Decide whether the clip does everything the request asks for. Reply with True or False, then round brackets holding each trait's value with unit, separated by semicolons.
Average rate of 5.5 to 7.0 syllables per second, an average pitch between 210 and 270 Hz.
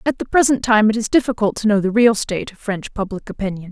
True (6.4 syllables/s; 215 Hz)